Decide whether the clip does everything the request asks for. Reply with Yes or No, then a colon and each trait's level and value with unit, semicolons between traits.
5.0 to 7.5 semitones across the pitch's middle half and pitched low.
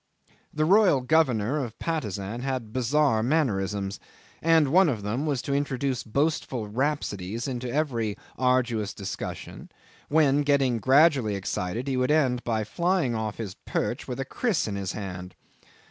Yes: average, 5.3 semitones; low, 125 Hz